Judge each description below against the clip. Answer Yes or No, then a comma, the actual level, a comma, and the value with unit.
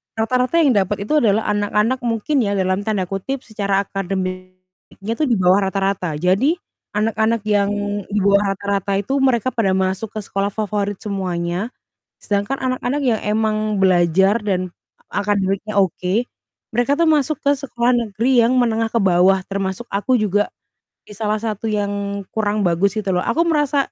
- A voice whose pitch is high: Yes, high, 205 Hz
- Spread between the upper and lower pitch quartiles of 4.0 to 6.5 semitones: No, average, 3.0 semitones